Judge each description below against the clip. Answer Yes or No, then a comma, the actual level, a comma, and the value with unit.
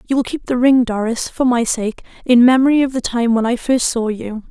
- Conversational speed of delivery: No, fast, 255 wpm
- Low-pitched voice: No, high, 240 Hz